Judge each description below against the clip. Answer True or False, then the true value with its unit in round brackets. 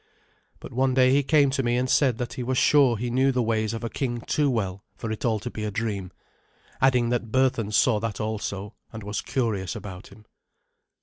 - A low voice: True (115 Hz)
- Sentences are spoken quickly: True (220 wpm)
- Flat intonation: False (3.3 semitones)